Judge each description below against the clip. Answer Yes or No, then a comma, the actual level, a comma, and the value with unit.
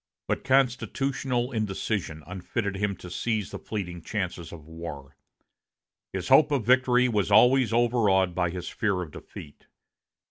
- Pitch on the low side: Yes, low, 105 Hz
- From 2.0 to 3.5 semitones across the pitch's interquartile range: No, wide, 5.6 semitones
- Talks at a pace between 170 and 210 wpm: No, average, 140 wpm